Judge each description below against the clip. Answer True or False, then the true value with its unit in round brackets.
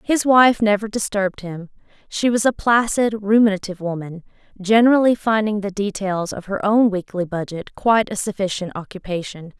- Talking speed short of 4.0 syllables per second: False (5.3 syllables/s)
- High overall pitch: True (205 Hz)